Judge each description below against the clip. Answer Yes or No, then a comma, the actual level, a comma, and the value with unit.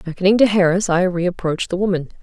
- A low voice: No, medium, 185 Hz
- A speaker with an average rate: Yes, average, 190 wpm